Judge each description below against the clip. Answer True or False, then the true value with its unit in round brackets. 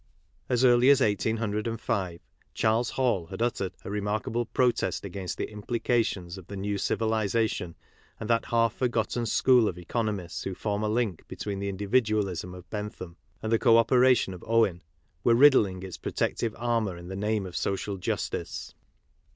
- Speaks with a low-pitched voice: True (105 Hz)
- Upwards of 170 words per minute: False (160 wpm)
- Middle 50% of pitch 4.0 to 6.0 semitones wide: False (3.3 semitones)